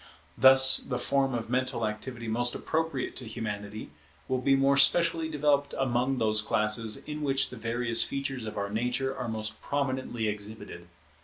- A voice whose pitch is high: No, low, 125 Hz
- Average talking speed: Yes, average, 160 wpm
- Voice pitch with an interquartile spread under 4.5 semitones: Yes, average, 3.6 semitones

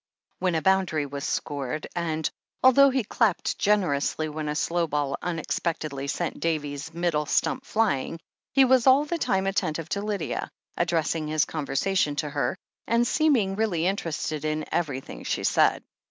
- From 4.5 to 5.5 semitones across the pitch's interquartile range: Yes, average, 4.9 semitones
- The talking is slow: No, average, 155 wpm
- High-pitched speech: No, medium, 165 Hz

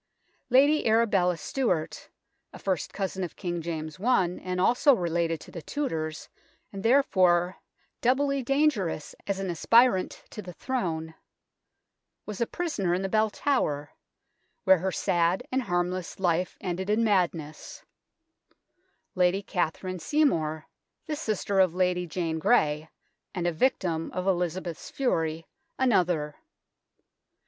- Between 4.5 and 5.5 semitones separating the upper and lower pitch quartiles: Yes, average, 4.8 semitones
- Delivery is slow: Yes, slow, 125 wpm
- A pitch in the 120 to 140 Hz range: No, medium, 185 Hz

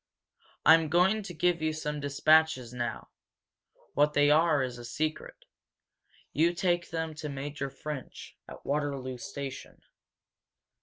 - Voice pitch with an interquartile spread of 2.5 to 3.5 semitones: Yes, average, 2.8 semitones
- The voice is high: No, medium, 150 Hz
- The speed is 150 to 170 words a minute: No, slow, 135 wpm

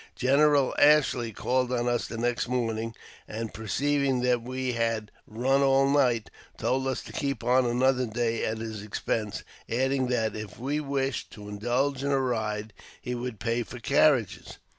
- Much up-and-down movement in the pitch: No, average, 2.9 semitones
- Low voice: Yes, low, 125 Hz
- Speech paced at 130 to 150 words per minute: No, average, 165 wpm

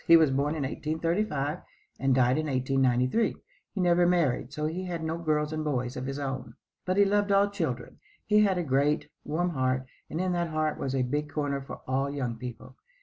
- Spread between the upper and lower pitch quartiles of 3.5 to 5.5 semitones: Yes, average, 4.6 semitones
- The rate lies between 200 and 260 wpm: Yes, fast, 205 wpm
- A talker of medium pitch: Yes, medium, 150 Hz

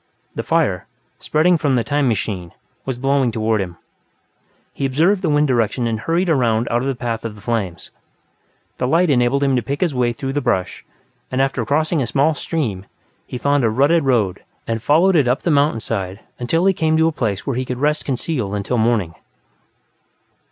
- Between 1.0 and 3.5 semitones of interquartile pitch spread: No, average, 4.6 semitones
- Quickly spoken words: No, average, 195 wpm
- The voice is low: Yes, low, 130 Hz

